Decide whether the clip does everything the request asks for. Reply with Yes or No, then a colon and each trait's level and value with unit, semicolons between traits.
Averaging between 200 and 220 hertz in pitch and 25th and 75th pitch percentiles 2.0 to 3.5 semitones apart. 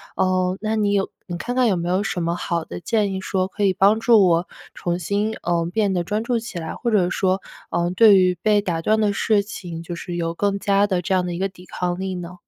No: high, 190 Hz; average, 2.8 semitones